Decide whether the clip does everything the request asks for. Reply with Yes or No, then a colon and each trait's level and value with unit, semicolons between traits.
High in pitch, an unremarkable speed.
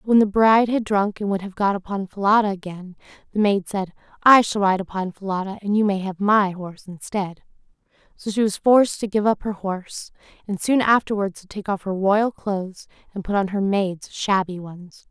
No: high, 200 Hz; fast, 210 wpm